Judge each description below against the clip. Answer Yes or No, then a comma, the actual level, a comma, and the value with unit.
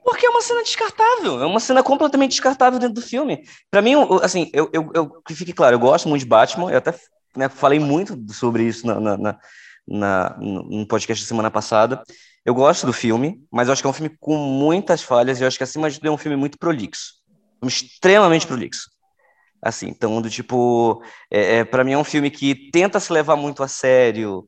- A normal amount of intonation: No, wide, 7.0 semitones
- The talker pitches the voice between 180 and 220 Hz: No, medium, 145 Hz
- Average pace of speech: No, fast, 215 wpm